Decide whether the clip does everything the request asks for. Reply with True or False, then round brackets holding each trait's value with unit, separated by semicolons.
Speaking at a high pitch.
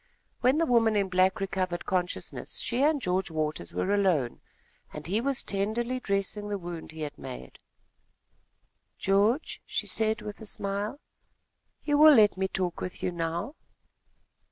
True (195 Hz)